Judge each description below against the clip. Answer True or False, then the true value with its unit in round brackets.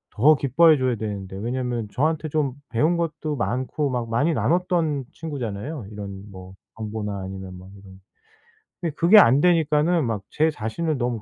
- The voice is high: False (130 Hz)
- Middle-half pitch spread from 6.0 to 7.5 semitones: True (6.7 semitones)